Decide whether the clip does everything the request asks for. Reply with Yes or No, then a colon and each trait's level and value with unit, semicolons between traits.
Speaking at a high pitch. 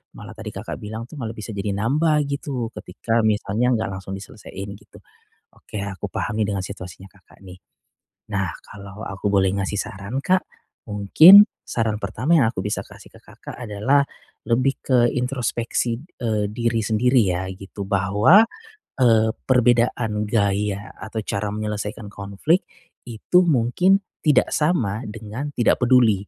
No: low, 110 Hz